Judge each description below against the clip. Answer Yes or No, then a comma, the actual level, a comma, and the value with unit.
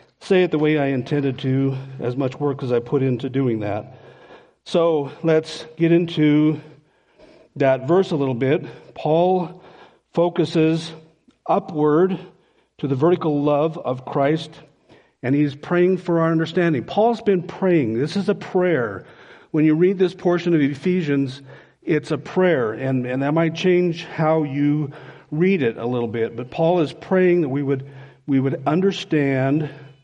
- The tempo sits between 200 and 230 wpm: No, average, 165 wpm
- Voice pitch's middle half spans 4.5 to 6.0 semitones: No, average, 3.9 semitones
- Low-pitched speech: No, medium, 155 Hz